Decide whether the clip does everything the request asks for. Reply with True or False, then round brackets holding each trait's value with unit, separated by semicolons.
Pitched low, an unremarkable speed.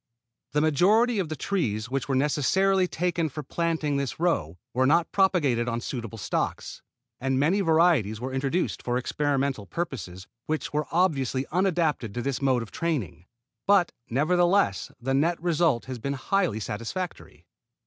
False (145 Hz; 150 wpm)